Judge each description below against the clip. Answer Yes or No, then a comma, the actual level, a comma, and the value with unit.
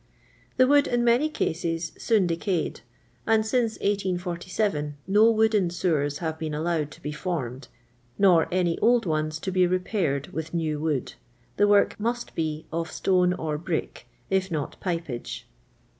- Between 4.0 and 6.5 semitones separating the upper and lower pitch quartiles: Yes, average, 4.5 semitones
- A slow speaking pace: No, average, 155 wpm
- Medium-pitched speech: Yes, medium, 175 Hz